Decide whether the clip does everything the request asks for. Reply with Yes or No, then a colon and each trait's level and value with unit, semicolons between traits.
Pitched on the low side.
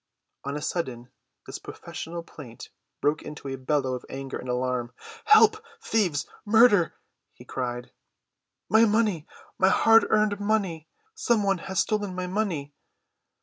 No: medium, 170 Hz